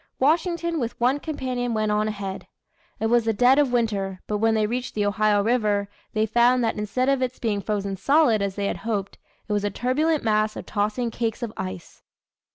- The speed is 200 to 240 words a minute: Yes, fast, 205 wpm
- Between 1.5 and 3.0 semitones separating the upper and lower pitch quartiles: No, average, 3.4 semitones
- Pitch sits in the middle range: No, high, 225 Hz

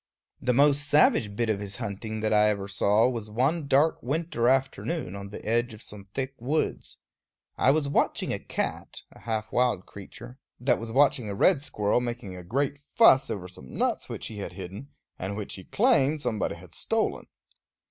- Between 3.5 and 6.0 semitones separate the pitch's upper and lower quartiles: Yes, average, 5.2 semitones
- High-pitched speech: No, low, 120 Hz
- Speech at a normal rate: Yes, average, 190 wpm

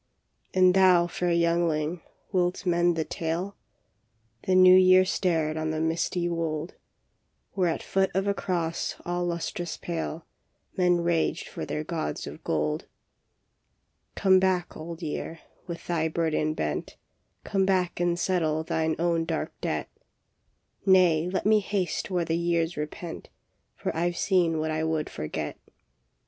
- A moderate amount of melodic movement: No, narrow, 2.2 semitones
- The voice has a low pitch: No, medium, 170 Hz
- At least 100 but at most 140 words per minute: No, average, 155 wpm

